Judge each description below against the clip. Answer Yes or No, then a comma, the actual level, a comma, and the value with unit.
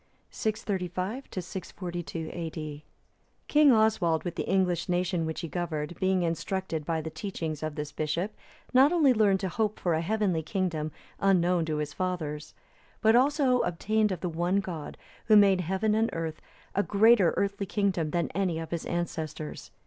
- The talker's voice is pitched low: No, medium, 180 Hz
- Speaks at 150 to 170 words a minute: Yes, average, 165 wpm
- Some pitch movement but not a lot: Yes, average, 3.8 semitones